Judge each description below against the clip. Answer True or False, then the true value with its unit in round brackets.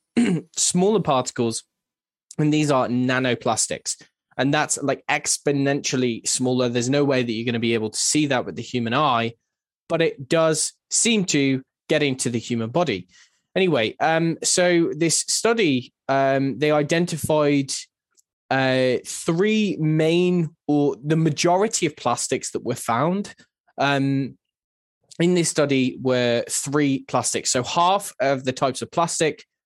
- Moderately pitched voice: True (145 Hz)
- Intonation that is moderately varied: True (4.6 semitones)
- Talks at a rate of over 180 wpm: False (140 wpm)